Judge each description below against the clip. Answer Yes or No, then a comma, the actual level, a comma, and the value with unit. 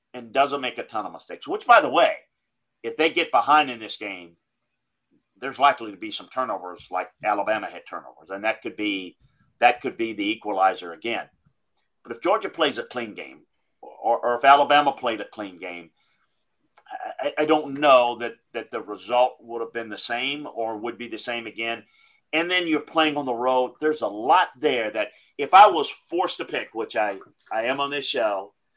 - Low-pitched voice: Yes, low, 125 Hz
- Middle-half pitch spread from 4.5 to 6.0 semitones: Yes, average, 5.0 semitones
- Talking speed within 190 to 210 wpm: Yes, average, 200 wpm